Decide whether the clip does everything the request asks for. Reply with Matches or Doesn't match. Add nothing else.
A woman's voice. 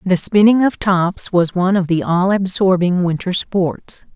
Matches